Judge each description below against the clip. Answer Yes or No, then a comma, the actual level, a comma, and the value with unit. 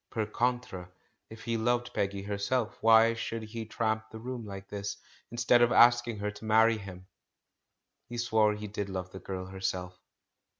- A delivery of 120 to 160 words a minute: No, average, 170 wpm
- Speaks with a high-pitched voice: No, low, 110 Hz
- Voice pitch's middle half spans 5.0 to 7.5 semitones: No, average, 2.8 semitones